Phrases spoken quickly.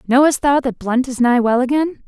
Yes: fast, 230 wpm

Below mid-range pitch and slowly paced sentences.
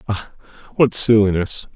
Yes: low, 105 Hz; slow, 105 wpm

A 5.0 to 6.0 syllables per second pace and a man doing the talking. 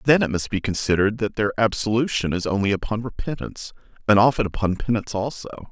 No: 6.4 syllables/s; male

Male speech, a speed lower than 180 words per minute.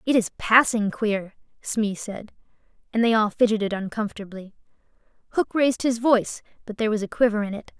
No: female; average, 170 wpm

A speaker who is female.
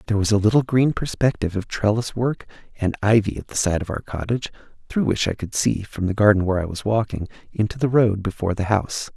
No: male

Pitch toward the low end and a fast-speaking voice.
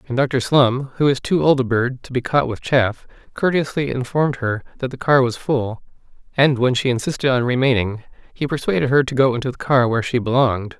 Yes: low, 130 Hz; fast, 210 wpm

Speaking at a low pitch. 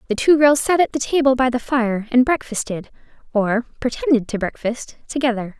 No: very high, 250 Hz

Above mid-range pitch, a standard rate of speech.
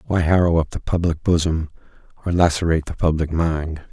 No: very low, 80 Hz; average, 170 wpm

